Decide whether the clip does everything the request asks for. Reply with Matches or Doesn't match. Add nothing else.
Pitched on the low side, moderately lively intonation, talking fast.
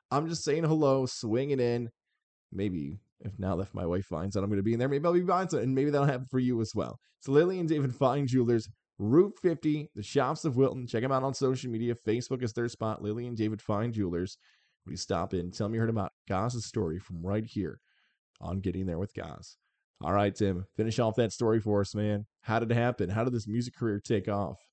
Matches